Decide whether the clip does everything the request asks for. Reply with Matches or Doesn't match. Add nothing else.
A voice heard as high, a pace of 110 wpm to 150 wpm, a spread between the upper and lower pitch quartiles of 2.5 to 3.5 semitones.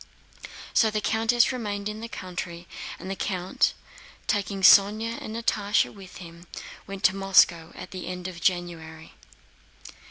Matches